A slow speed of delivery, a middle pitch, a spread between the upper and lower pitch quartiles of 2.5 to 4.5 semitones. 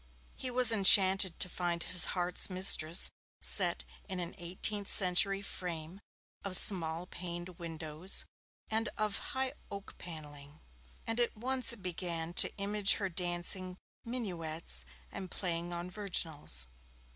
Yes: slow, 125 wpm; medium, 180 Hz; average, 2.9 semitones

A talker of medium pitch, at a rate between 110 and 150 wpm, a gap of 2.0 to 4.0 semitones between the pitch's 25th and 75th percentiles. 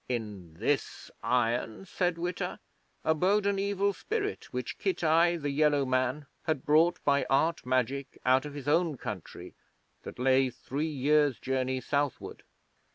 No: medium, 145 Hz; average, 140 wpm; average, 4.6 semitones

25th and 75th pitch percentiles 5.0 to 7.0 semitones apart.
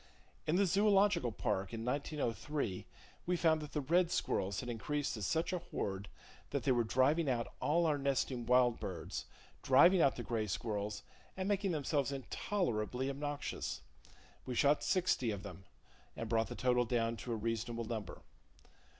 Yes: average, 5.3 semitones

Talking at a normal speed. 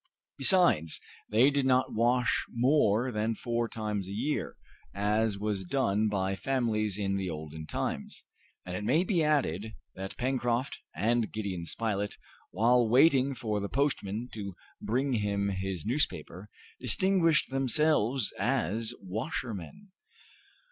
No: slow, 125 wpm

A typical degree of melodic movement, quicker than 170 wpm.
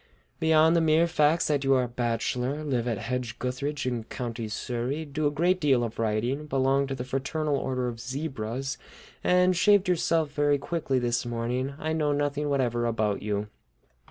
Yes: average, 4.0 semitones; average, 180 wpm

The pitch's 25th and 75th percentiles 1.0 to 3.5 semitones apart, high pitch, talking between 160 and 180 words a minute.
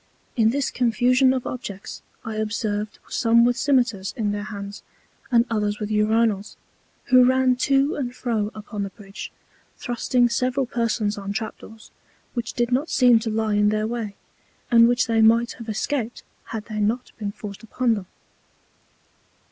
Yes: narrow, 2.6 semitones; high, 225 Hz; average, 165 wpm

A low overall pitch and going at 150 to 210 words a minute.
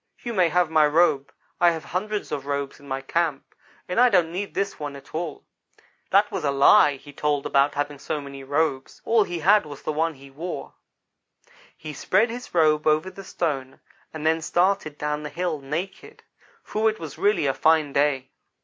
No: medium, 155 Hz; average, 195 wpm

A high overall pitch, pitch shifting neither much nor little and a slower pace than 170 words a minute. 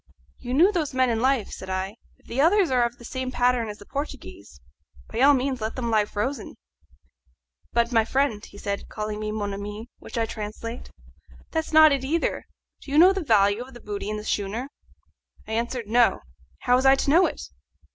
No: high, 240 Hz; average, 4.2 semitones; fast, 205 wpm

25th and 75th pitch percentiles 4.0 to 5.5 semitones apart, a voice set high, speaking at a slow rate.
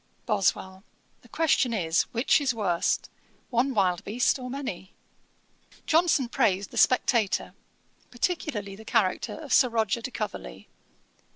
Yes: average, 5.1 semitones; high, 230 Hz; slow, 125 wpm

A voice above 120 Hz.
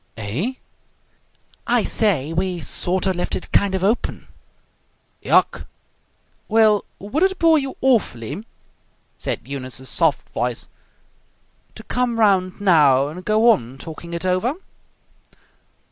Yes: medium, 185 Hz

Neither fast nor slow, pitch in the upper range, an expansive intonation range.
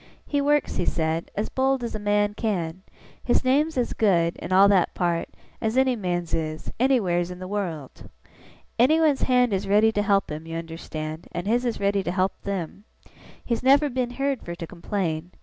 Yes: average, 190 wpm; high, 200 Hz; wide, 6.1 semitones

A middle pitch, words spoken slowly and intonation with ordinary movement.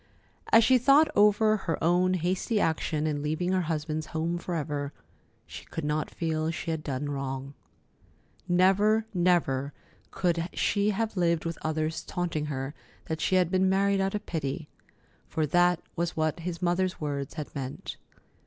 No: medium, 170 Hz; average, 155 wpm; average, 3.4 semitones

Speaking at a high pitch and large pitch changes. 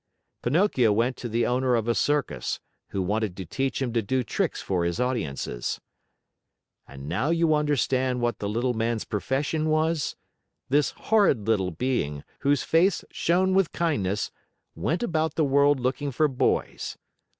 No: low, 130 Hz; wide, 5.7 semitones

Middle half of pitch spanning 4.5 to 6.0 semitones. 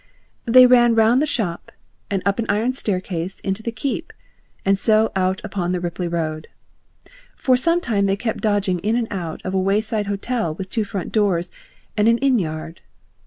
No: average, 3.8 semitones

